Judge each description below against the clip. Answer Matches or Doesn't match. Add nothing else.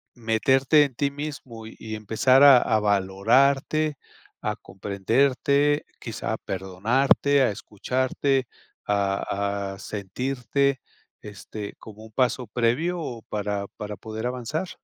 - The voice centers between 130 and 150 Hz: Doesn't match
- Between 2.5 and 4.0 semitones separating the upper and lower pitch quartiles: Doesn't match